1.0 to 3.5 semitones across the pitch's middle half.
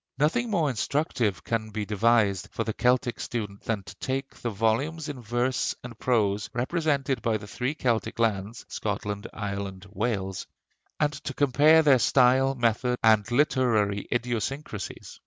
No: average, 4.2 semitones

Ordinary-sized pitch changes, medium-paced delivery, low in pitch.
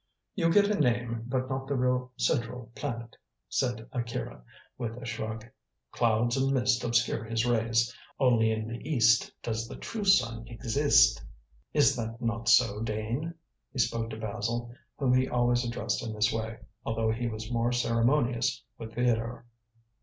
No: narrow, 1.8 semitones; average, 160 wpm; low, 120 Hz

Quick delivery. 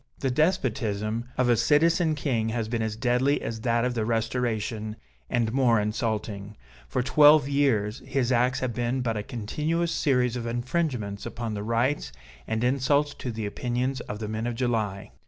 No: average, 175 wpm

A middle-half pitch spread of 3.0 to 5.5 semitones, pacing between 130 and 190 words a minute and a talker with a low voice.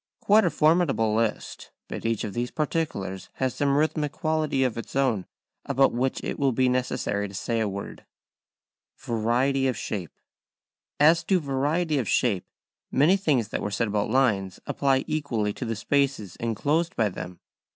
Yes: average, 5.2 semitones; average, 170 wpm; low, 130 Hz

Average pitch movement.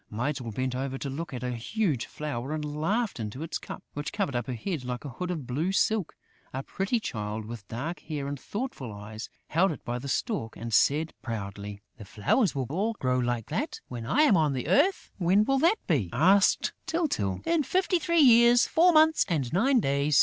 No: wide, 9.0 semitones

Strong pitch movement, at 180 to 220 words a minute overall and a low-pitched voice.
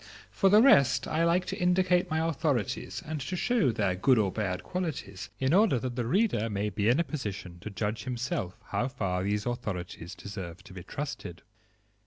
Yes: wide, 8.3 semitones; average, 190 wpm; low, 120 Hz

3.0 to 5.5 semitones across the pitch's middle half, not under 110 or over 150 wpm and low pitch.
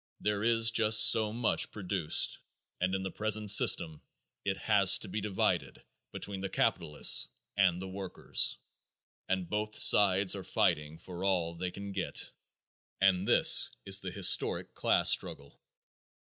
No: narrow, 2.4 semitones; average, 145 wpm; very low, 95 Hz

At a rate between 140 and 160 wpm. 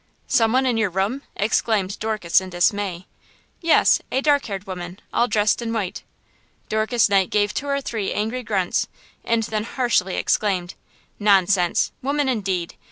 Yes: average, 155 wpm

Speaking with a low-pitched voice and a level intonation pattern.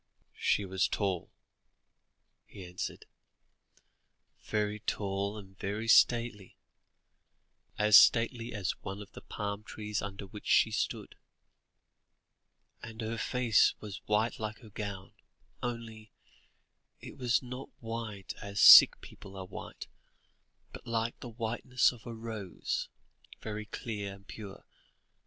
Yes: low, 105 Hz; narrow, 2.3 semitones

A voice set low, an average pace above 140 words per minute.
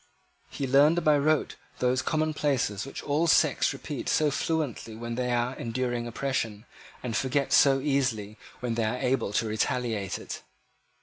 Yes: low, 125 Hz; average, 150 wpm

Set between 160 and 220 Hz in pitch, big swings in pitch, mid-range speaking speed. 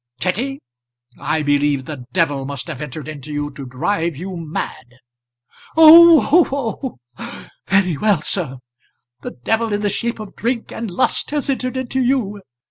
Yes: medium, 185 Hz; wide, 8.8 semitones; average, 155 wpm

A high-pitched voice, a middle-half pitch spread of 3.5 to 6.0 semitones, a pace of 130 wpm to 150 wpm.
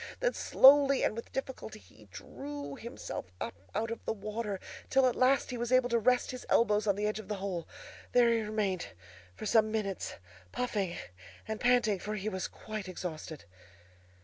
No: high, 215 Hz; average, 4.1 semitones; average, 180 wpm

